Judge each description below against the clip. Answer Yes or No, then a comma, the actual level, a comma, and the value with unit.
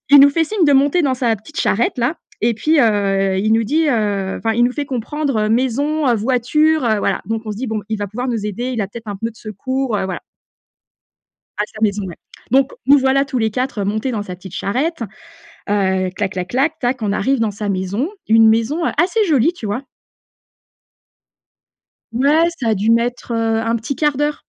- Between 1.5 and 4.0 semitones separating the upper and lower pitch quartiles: No, average, 4.6 semitones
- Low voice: No, high, 230 Hz